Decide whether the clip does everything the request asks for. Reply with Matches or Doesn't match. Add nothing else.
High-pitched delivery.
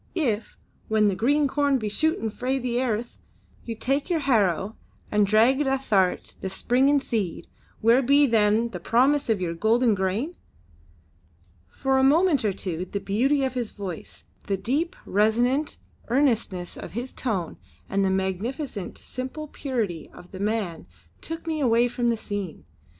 Matches